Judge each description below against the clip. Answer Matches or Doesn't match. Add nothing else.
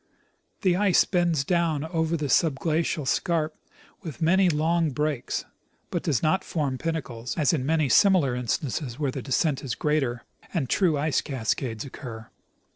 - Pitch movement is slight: Doesn't match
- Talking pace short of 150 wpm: Doesn't match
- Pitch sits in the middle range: Matches